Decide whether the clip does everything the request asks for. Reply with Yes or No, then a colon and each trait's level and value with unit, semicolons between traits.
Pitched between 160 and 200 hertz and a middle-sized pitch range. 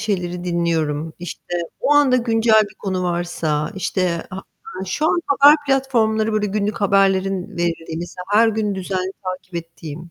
Yes: high, 190 Hz; average, 4.0 semitones